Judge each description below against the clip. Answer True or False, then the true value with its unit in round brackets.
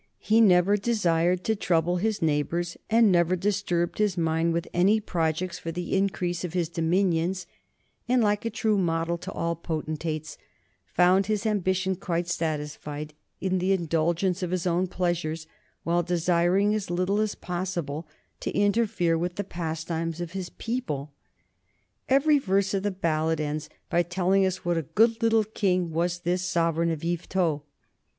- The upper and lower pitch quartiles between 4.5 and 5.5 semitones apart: False (2.8 semitones)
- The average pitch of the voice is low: False (175 Hz)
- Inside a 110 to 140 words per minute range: False (160 wpm)